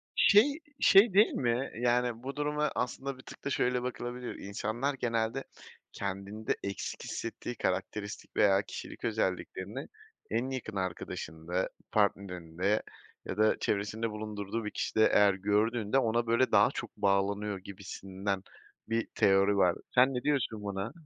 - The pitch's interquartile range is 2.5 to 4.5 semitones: Yes, average, 3.9 semitones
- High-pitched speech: No, low, 110 Hz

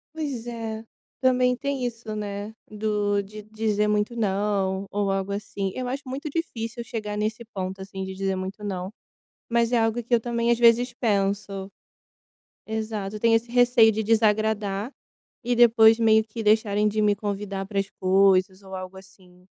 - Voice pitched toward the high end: Yes, high, 215 Hz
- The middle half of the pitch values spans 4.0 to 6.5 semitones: No, average, 2.7 semitones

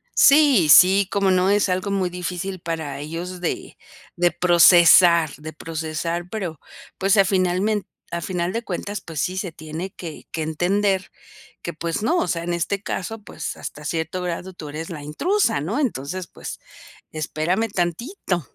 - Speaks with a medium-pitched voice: Yes, medium, 180 Hz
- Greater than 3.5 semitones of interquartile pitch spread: No, average, 3.1 semitones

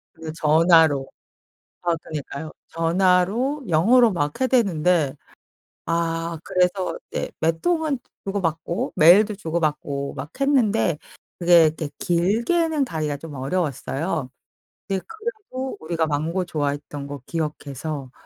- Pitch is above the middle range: No, medium, 165 Hz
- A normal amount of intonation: Yes, average, 4.7 semitones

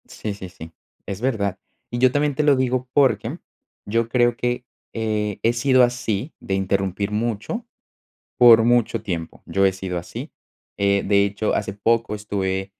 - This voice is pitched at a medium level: No, low, 110 Hz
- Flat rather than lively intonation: No, average, 3.7 semitones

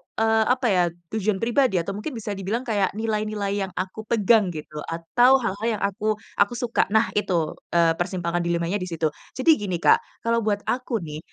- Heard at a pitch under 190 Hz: No, high, 205 Hz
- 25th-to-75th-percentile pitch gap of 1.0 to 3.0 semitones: No, average, 4.0 semitones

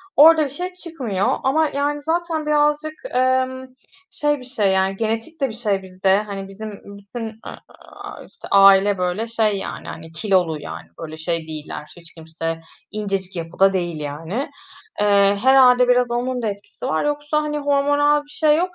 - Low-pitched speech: No, high, 220 Hz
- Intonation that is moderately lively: No, wide, 7.2 semitones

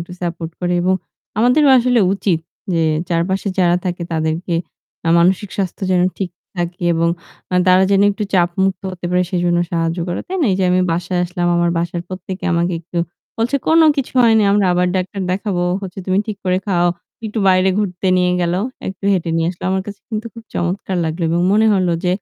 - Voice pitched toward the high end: No, medium, 180 Hz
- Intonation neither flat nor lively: No, narrow, 2.2 semitones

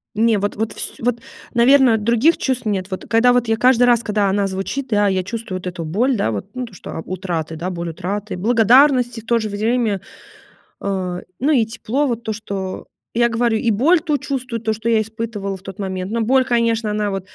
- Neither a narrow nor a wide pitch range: Yes, average, 3.6 semitones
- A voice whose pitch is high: Yes, high, 220 Hz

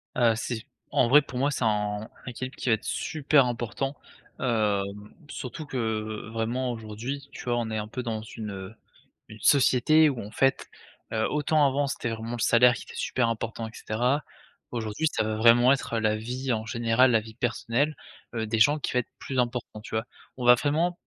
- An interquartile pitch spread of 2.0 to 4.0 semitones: Yes, average, 3.1 semitones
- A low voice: Yes, low, 120 Hz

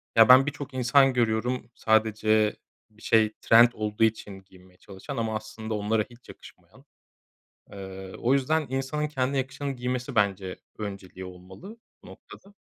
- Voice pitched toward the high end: No, low, 110 Hz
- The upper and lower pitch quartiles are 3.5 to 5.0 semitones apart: Yes, average, 4.0 semitones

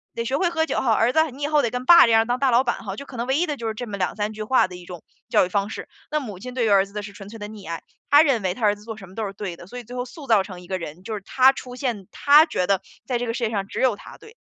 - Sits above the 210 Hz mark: Yes, high, 225 Hz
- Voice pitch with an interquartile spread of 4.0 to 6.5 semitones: Yes, average, 4.5 semitones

